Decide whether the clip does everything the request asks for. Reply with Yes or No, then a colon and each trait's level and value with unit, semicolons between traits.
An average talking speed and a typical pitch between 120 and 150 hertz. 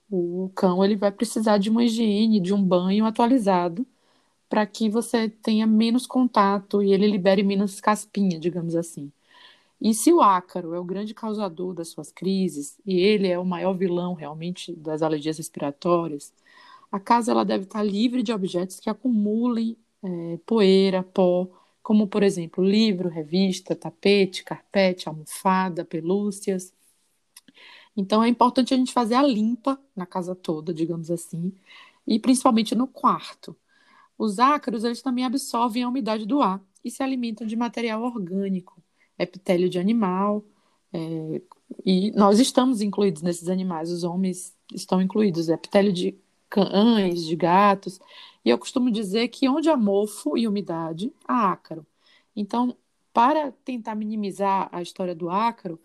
No: average, 150 wpm; high, 200 Hz